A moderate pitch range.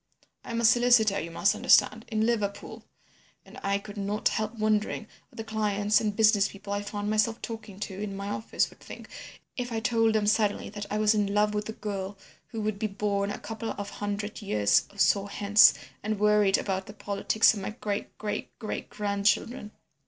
No: narrow, 1.4 semitones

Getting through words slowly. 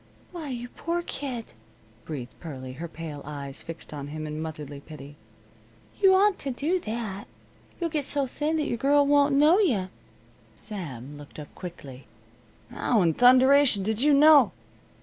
No: average, 155 wpm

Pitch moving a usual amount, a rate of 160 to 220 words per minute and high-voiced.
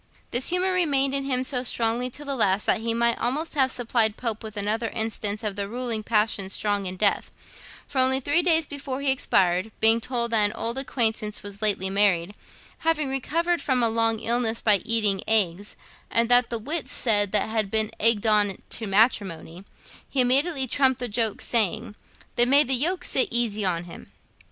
Yes: average, 3.9 semitones; average, 195 wpm; high, 230 Hz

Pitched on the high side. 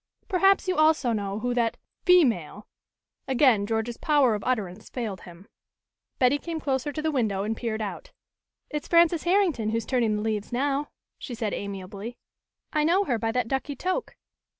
Yes: high, 245 Hz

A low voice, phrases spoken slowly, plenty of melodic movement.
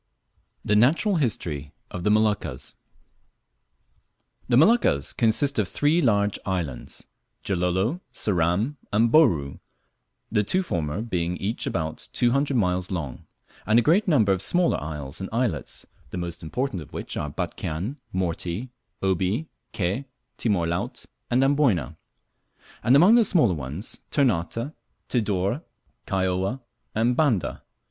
Yes: low, 105 Hz; slow, 130 wpm; wide, 6.8 semitones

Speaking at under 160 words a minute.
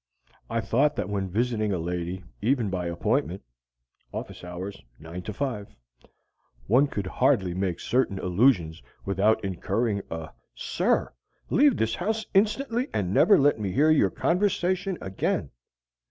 Yes: slow, 135 wpm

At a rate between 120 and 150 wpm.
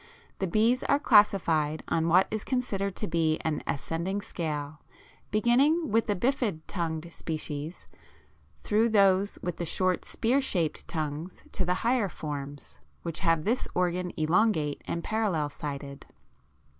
Yes: average, 140 wpm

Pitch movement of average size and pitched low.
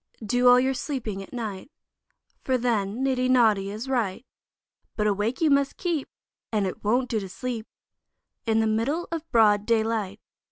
No: average, 3.5 semitones; high, 230 Hz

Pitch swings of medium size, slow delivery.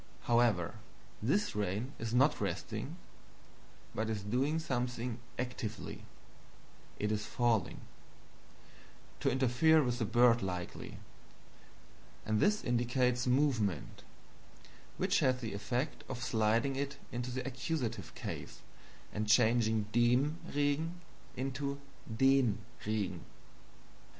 Yes: average, 3.5 semitones; slow, 105 wpm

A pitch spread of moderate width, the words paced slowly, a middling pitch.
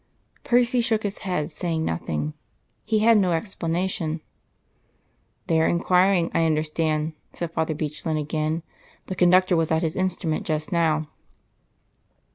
Yes: average, 3.0 semitones; slow, 130 wpm; medium, 165 Hz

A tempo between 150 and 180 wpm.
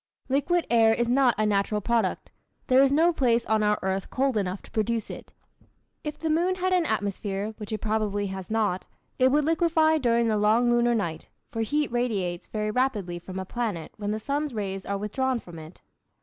No: average, 200 wpm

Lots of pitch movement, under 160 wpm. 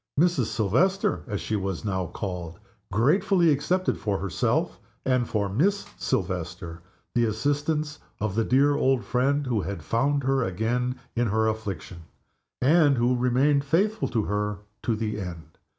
Yes: wide, 6.1 semitones; average, 150 wpm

